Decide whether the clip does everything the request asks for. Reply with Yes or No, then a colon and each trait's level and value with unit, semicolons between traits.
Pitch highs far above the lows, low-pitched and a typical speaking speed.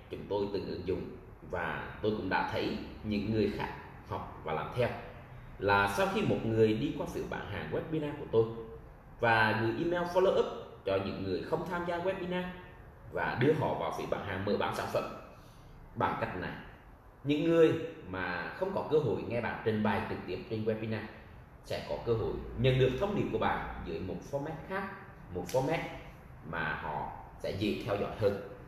Yes: wide, 6.8 semitones; low, 125 Hz; average, 195 wpm